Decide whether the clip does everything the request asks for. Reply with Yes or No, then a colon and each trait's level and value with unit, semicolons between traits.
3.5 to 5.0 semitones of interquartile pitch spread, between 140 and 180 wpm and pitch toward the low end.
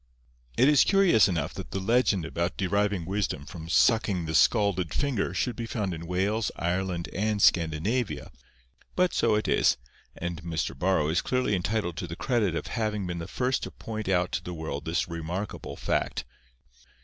Yes: average, 4.4 semitones; average, 175 wpm; very low, 95 Hz